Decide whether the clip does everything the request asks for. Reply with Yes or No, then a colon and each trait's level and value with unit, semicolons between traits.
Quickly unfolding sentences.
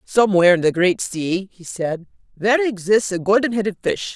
No: average, 190 wpm